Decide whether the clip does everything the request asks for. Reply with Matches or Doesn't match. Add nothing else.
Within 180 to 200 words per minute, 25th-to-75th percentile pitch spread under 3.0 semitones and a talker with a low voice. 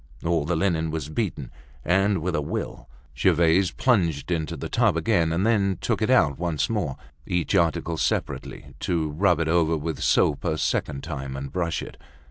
Matches